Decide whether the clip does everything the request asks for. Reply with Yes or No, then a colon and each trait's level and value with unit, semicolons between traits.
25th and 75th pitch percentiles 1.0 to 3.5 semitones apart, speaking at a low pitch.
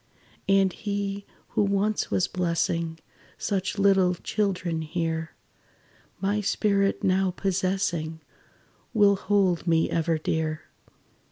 No: average, 3.1 semitones; medium, 185 Hz